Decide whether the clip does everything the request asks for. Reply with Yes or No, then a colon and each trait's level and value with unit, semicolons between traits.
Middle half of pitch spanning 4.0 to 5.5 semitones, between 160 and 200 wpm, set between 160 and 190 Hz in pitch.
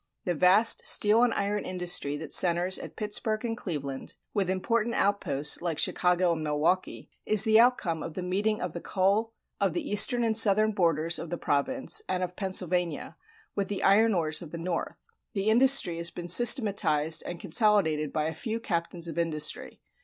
Yes: average, 4.3 semitones; average, 180 wpm; medium, 185 Hz